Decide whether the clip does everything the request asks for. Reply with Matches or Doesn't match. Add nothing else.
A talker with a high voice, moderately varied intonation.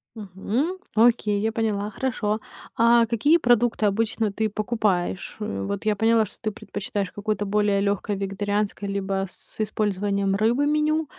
Doesn't match